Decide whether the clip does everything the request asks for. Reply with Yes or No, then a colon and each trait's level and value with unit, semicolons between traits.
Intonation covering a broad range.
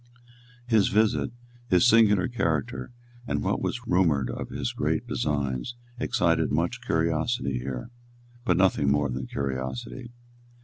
Yes: wide, 8.1 semitones